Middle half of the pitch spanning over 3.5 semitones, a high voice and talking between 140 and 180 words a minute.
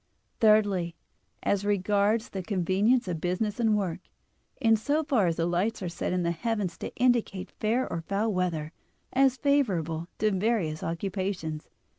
Yes: average, 4.3 semitones; high, 200 Hz; average, 155 wpm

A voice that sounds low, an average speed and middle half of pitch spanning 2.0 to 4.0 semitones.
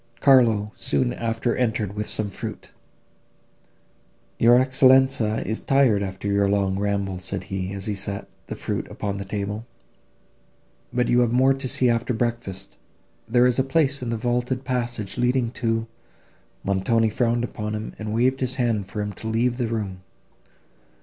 Yes: low, 115 Hz; average, 165 wpm; average, 3.4 semitones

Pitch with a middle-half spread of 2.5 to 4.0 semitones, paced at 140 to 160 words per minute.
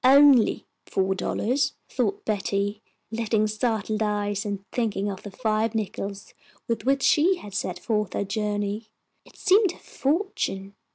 Yes: average, 3.6 semitones; average, 150 wpm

